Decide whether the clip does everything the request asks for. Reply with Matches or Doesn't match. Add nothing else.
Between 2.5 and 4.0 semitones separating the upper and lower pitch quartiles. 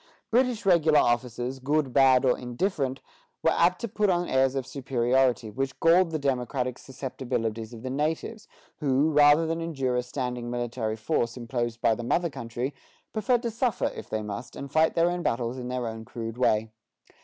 Doesn't match